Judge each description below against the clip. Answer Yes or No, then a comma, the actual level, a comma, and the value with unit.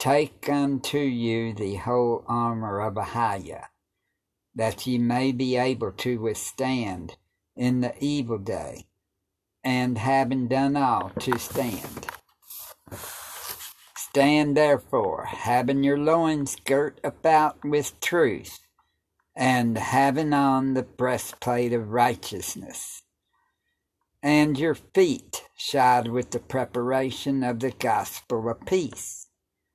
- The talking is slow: Yes, slow, 105 wpm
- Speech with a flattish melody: No, average, 3.4 semitones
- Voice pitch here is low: Yes, low, 125 Hz